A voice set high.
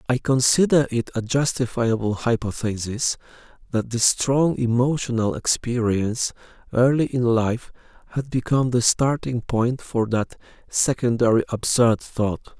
No: low, 120 Hz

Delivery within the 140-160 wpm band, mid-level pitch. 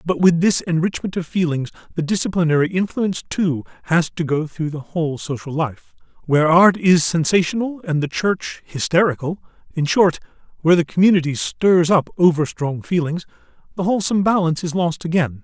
Yes: average, 150 wpm; medium, 170 Hz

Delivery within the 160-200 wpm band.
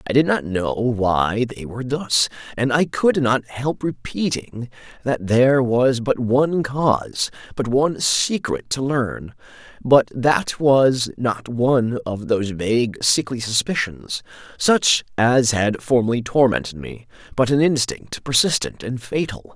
No: average, 145 wpm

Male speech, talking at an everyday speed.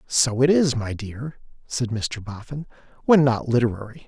Yes: male; average, 160 wpm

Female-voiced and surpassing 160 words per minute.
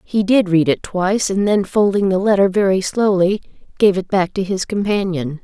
Yes: female; average, 200 wpm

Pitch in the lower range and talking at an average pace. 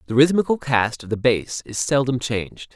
Yes: low, 125 Hz; average, 195 wpm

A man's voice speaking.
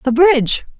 No: female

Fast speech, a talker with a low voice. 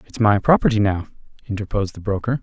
No: average, 175 wpm; low, 105 Hz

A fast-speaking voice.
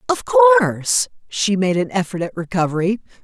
No: average, 150 wpm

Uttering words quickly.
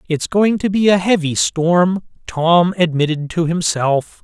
No: average, 155 wpm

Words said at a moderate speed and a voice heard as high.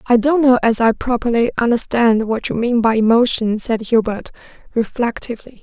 Yes: average, 160 wpm; high, 235 Hz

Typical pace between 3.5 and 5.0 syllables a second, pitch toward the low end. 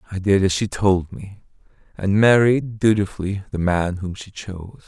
Yes: 4.7 syllables/s; low, 100 Hz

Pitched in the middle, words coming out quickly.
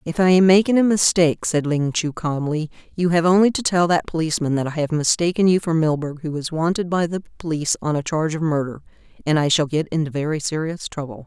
Yes: medium, 160 Hz; fast, 230 wpm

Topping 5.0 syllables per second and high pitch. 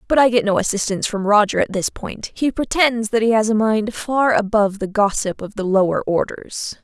Yes: 5.3 syllables/s; high, 220 Hz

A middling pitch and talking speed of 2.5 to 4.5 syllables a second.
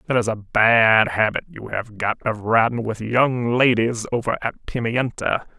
No: low, 115 Hz; 4.4 syllables/s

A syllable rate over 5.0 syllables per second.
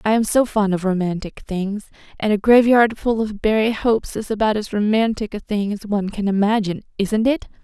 Yes: 5.5 syllables/s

